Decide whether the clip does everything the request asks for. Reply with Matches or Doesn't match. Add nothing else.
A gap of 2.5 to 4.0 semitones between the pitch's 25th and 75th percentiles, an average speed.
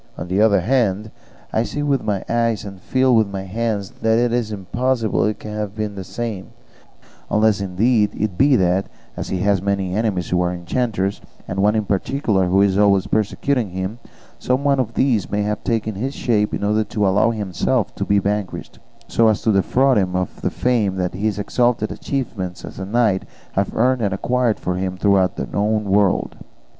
Matches